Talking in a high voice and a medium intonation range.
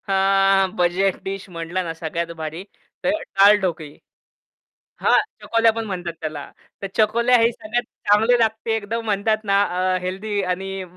Yes: high, 195 Hz; average, 3.3 semitones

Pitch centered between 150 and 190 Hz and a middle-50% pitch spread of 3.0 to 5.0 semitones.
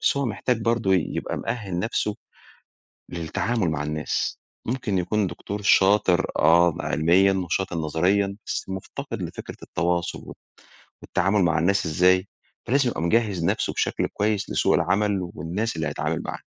No: very low, 95 Hz; average, 3.6 semitones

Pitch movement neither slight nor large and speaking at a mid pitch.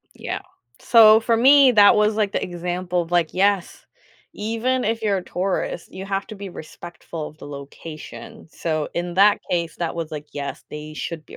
Yes: average, 4.4 semitones; medium, 180 Hz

